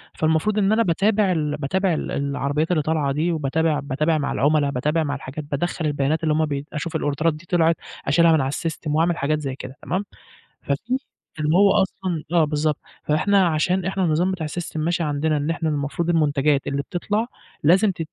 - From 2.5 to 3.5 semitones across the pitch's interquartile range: Yes, average, 2.9 semitones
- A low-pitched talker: No, medium, 155 Hz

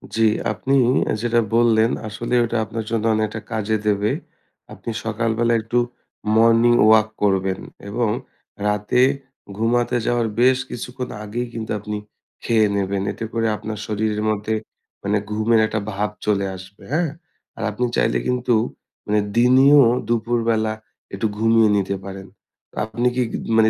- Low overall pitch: Yes, low, 110 Hz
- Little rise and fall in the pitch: Yes, narrow, 2.0 semitones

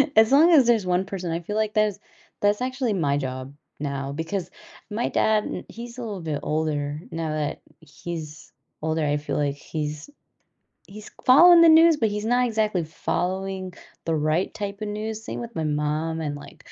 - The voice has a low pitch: No, medium, 185 Hz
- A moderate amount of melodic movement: No, wide, 6.1 semitones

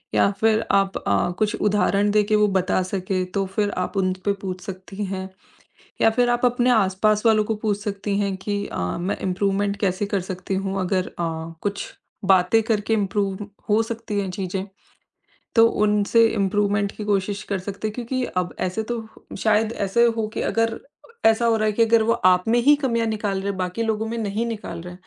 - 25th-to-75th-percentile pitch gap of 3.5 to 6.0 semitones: No, narrow, 2.5 semitones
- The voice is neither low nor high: No, high, 205 Hz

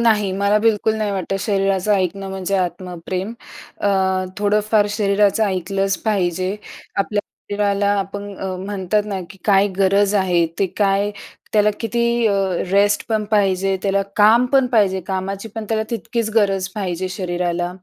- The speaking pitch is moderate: No, high, 200 Hz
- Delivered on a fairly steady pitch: Yes, narrow, 1.7 semitones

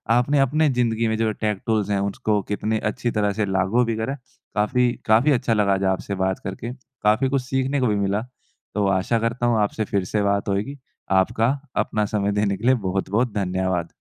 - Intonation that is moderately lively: Yes, average, 3.5 semitones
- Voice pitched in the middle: No, low, 110 Hz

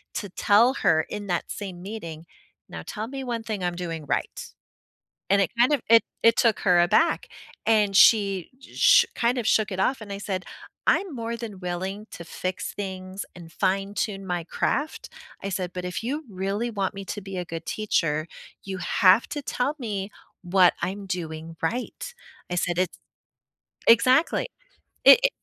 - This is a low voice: No, high, 195 Hz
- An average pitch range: Yes, average, 4.1 semitones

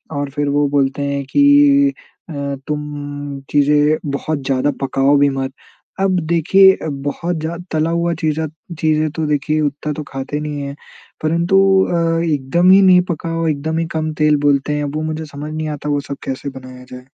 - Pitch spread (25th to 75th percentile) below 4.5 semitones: Yes, narrow, 2.4 semitones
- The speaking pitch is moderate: Yes, medium, 150 Hz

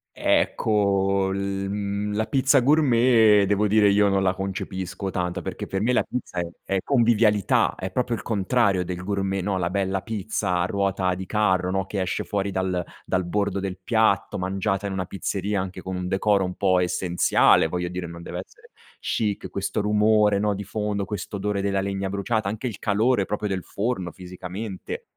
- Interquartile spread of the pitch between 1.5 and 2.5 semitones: Yes, narrow, 2.0 semitones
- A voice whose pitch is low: Yes, low, 100 Hz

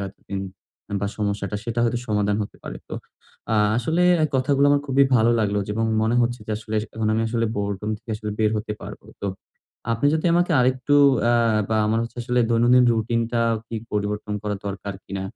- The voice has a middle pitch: No, low, 115 Hz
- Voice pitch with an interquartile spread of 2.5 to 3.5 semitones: Yes, average, 2.8 semitones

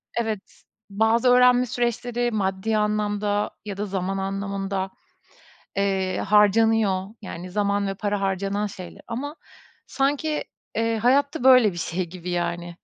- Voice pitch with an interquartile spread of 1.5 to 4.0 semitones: Yes, average, 3.0 semitones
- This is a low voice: No, high, 205 Hz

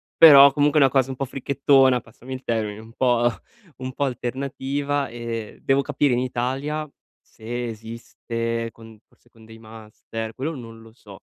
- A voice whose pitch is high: No, low, 125 Hz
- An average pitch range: Yes, average, 3.2 semitones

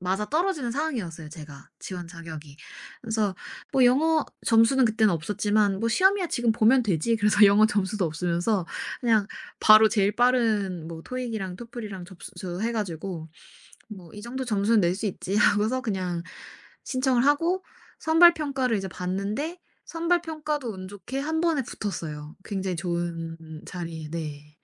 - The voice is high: Yes, high, 210 Hz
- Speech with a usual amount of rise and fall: No, wide, 6.0 semitones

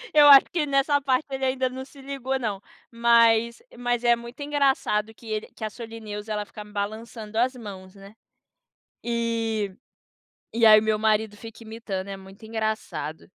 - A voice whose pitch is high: Yes, high, 225 Hz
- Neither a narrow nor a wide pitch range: Yes, average, 3.2 semitones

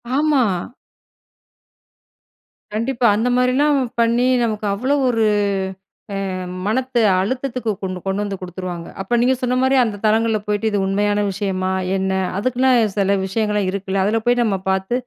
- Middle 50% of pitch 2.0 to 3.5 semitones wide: No, average, 4.2 semitones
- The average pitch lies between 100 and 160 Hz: No, high, 215 Hz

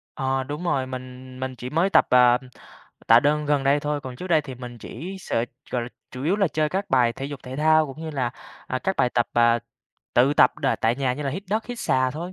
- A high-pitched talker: No, low, 135 Hz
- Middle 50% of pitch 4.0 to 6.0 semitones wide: No, average, 3.4 semitones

